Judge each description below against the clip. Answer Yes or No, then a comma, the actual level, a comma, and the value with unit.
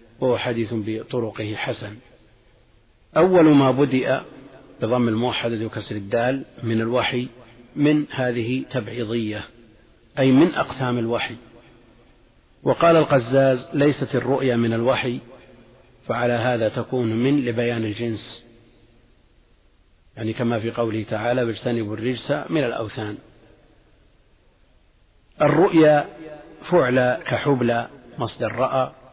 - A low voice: Yes, low, 120 Hz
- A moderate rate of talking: Yes, average, 95 wpm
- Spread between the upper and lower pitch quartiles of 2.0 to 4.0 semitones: Yes, narrow, 2.5 semitones